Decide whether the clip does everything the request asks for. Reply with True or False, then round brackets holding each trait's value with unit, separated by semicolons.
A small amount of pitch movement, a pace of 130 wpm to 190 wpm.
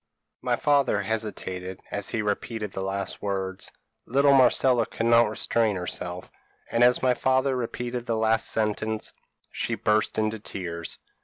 False (3.5 semitones; 150 wpm)